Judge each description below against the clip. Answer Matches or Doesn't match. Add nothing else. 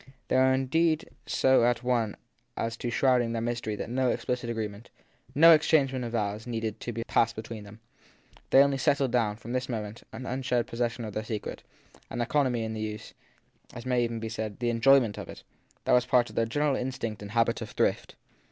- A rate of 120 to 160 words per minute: Doesn't match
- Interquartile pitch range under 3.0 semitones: Matches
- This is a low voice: Matches